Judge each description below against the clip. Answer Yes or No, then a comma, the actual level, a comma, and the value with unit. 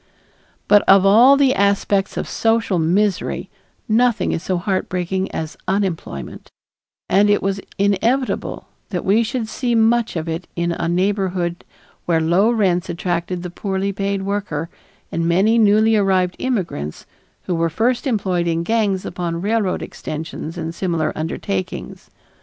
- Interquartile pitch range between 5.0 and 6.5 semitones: No, average, 3.7 semitones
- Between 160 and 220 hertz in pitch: Yes, high, 190 Hz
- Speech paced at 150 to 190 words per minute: No, average, 140 wpm